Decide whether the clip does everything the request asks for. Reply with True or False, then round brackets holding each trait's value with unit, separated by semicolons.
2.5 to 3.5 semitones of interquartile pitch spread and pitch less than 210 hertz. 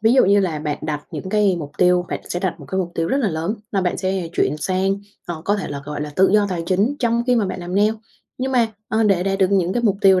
True (3.2 semitones; 190 Hz)